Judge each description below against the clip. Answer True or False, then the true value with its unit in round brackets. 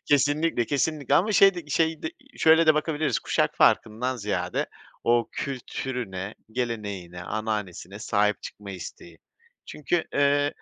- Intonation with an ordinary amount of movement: False (6.5 semitones)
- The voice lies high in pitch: False (125 Hz)